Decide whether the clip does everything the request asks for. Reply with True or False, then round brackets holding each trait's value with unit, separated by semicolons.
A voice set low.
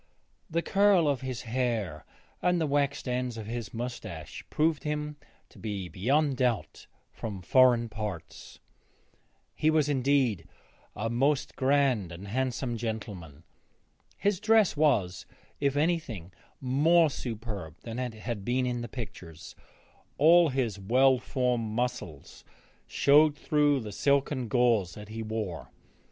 True (125 Hz)